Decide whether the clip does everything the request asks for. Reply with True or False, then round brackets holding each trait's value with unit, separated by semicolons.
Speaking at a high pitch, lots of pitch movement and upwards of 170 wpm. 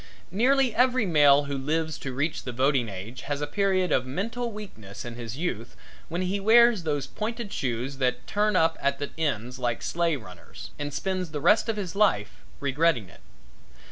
False (150 Hz; 7.5 semitones; 185 wpm)